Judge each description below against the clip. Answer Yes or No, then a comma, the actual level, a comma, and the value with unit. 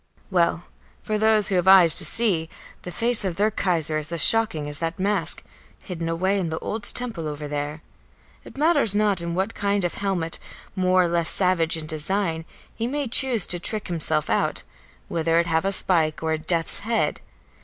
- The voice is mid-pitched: Yes, medium, 180 Hz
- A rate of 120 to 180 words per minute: No, average, 195 wpm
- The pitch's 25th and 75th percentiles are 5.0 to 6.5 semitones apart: No, average, 4.0 semitones